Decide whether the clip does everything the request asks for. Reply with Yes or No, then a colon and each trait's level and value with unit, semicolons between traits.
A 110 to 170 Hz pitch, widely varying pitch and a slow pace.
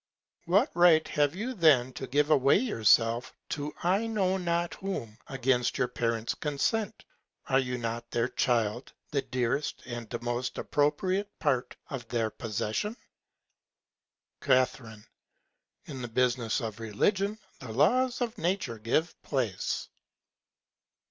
Yes: low, 135 Hz; wide, 6.8 semitones; slow, 125 wpm